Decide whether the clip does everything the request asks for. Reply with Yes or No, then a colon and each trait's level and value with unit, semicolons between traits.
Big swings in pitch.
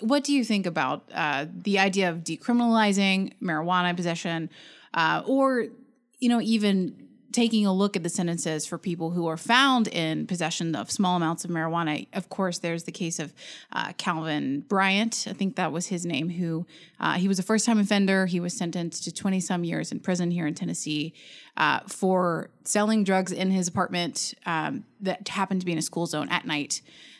No: average, 3.2 semitones